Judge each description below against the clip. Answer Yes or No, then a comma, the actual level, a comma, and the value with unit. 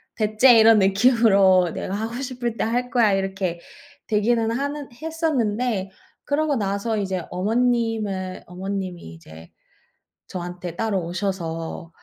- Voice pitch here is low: No, high, 210 Hz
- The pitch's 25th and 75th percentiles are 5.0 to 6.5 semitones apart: No, average, 4.1 semitones